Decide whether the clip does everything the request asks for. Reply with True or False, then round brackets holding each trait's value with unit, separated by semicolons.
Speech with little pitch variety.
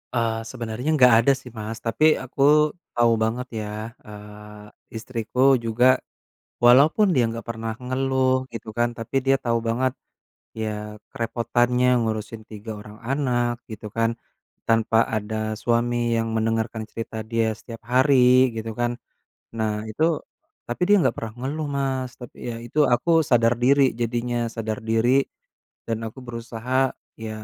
True (2.2 semitones)